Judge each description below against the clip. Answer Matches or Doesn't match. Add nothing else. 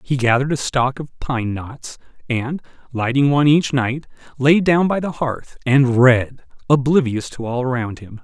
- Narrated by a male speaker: Matches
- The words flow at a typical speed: Matches